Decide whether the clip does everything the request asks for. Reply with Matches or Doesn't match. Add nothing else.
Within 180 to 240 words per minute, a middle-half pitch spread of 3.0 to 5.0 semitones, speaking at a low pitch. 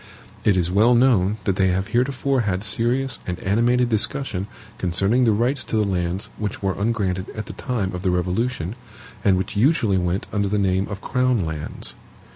Matches